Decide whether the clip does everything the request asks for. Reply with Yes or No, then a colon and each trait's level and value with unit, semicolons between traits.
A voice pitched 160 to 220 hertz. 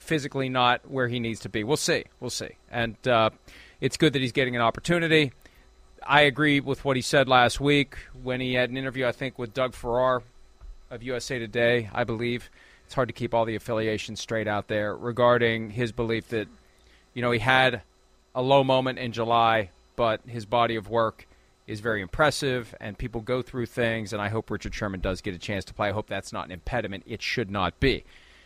No: low, 120 Hz